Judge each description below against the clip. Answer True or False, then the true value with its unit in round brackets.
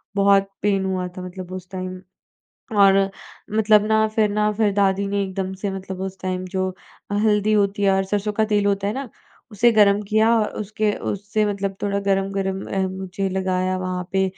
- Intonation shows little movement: True (1.6 semitones)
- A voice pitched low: False (195 Hz)